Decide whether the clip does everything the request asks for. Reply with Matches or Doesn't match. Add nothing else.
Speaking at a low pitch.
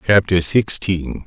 Matches